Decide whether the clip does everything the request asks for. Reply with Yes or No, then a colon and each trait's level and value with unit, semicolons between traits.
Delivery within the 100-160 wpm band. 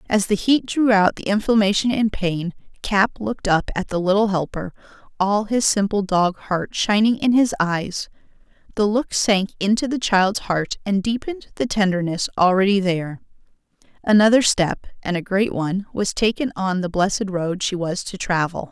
No: average, 175 wpm